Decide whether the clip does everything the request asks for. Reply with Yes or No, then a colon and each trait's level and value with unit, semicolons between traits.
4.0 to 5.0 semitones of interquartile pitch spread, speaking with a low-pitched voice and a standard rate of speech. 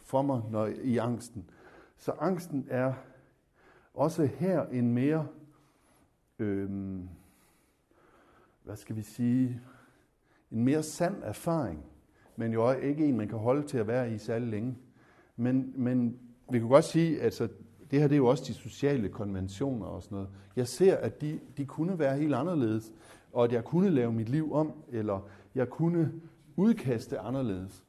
Yes: average, 4.6 semitones; low, 125 Hz; average, 165 wpm